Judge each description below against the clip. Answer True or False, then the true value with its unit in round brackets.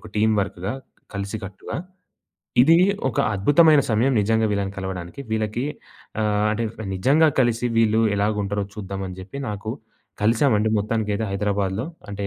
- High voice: False (105 Hz)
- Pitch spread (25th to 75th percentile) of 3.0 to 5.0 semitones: False (2.4 semitones)